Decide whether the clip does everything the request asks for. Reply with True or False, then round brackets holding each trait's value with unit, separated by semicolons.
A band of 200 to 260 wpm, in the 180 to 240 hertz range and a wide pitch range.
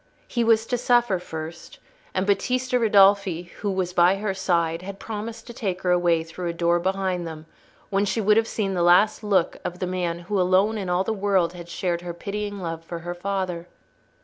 False (205 wpm; 185 Hz; 2.9 semitones)